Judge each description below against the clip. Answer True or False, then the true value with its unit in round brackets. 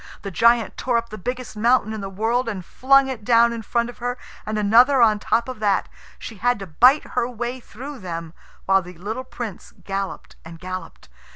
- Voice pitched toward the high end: True (230 Hz)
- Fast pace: True (210 wpm)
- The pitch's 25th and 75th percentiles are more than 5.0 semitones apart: False (3.8 semitones)